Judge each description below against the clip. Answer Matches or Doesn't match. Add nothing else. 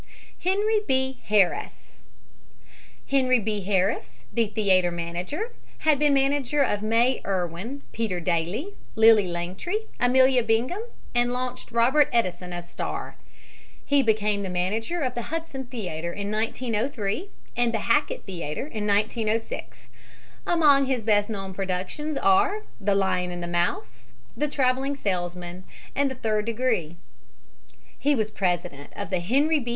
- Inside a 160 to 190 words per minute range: Doesn't match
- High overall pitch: Matches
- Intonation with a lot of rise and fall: Matches